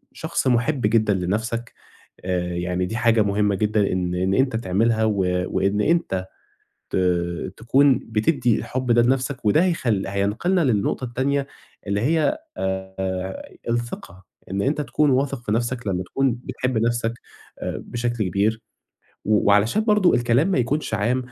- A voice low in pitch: Yes, low, 115 Hz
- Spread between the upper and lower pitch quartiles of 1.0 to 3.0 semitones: No, average, 4.4 semitones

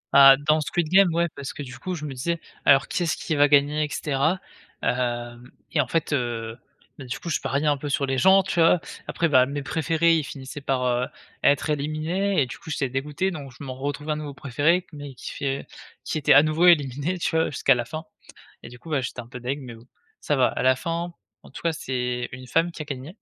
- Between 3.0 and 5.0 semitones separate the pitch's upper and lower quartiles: Yes, average, 3.7 semitones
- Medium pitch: Yes, medium, 145 Hz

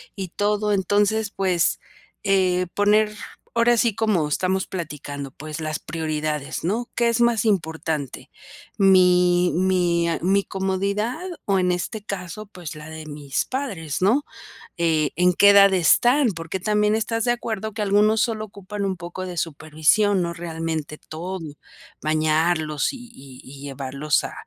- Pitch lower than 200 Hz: Yes, medium, 185 Hz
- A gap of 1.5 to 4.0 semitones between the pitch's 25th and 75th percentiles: No, average, 4.7 semitones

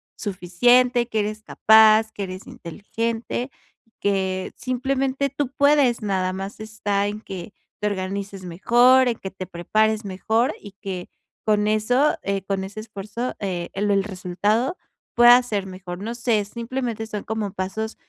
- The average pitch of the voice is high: Yes, high, 215 Hz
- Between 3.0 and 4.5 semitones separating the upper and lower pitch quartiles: Yes, average, 3.7 semitones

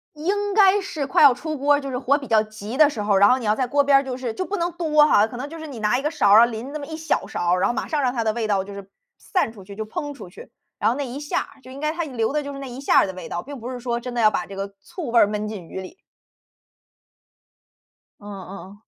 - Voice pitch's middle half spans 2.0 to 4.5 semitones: No, wide, 5.4 semitones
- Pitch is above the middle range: Yes, very high, 250 Hz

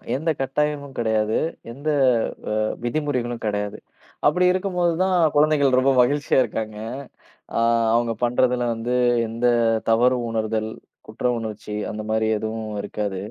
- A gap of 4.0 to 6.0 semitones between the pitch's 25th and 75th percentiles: Yes, average, 4.5 semitones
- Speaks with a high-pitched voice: No, low, 120 Hz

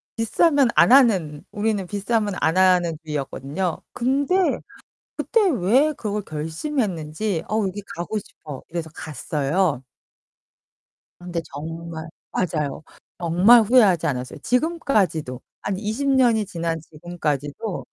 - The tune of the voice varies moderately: No, wide, 5.9 semitones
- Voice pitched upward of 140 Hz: Yes, medium, 185 Hz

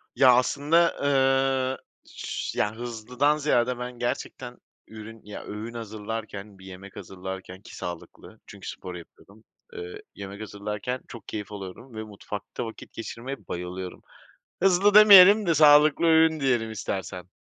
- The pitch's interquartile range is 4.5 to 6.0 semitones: Yes, wide, 5.6 semitones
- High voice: No, low, 115 Hz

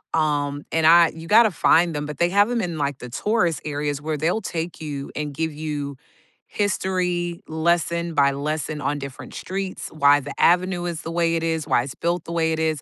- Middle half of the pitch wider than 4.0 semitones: No, average, 2.9 semitones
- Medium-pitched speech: Yes, medium, 160 Hz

